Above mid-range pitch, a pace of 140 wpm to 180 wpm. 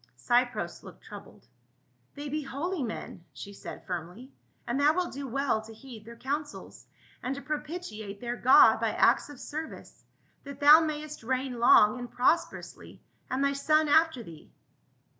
Yes: very high, 270 Hz; average, 170 wpm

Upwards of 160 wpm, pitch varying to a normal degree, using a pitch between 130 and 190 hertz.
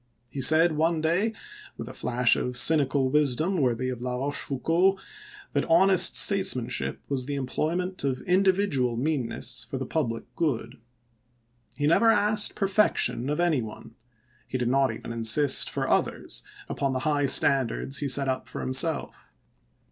No: average, 155 wpm; average, 4.7 semitones; medium, 140 Hz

